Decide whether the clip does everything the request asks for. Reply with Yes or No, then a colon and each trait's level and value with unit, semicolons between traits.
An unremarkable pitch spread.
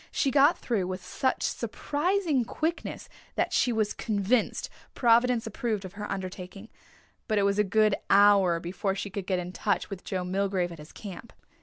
Yes: average, 3.9 semitones